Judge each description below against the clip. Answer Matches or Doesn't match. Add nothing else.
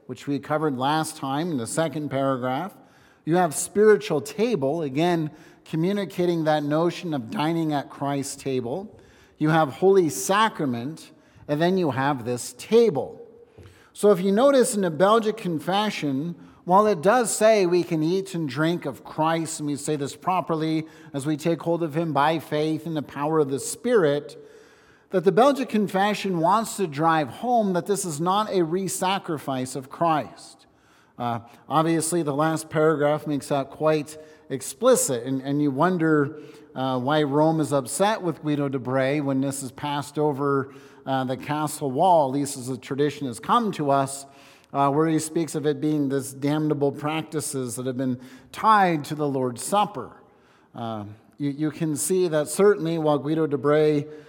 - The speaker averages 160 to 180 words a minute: Matches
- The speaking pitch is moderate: Matches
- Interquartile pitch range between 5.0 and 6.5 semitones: Doesn't match